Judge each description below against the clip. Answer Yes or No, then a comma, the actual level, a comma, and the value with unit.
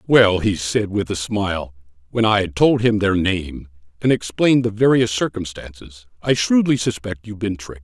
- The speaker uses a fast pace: No, average, 185 wpm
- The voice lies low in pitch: Yes, low, 100 Hz